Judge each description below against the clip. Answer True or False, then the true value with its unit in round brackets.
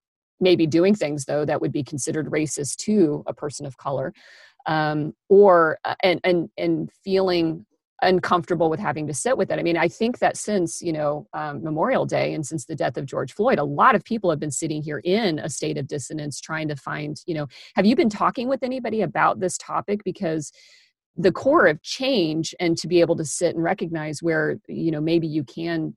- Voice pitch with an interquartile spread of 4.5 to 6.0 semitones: False (3.3 semitones)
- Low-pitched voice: False (165 Hz)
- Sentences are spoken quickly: True (210 wpm)